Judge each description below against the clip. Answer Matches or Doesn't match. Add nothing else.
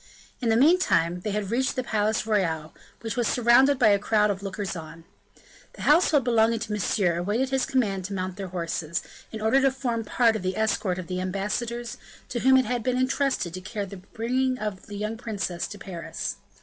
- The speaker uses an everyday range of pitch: Matches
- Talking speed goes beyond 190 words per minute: Matches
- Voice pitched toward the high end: Matches